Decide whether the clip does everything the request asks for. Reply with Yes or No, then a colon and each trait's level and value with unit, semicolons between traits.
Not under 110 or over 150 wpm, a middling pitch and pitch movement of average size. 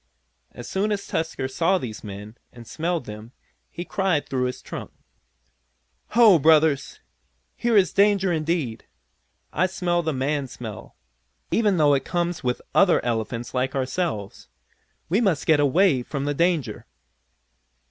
No: average, 140 wpm; medium, 155 Hz; wide, 6.1 semitones